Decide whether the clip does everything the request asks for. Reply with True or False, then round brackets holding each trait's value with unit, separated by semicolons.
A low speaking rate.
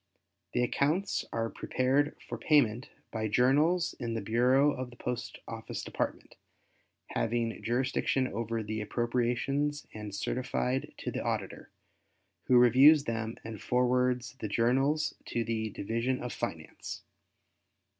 True (125 wpm)